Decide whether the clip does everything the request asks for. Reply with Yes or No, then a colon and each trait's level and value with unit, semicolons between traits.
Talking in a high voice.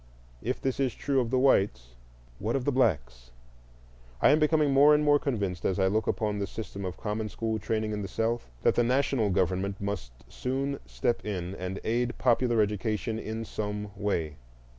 No: low, 110 Hz